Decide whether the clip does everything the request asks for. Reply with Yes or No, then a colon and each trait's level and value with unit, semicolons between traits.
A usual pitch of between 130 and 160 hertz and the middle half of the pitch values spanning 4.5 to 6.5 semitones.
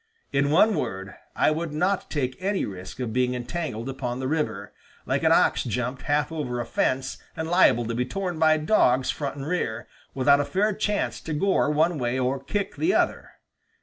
Yes: medium, 140 Hz; average, 4.8 semitones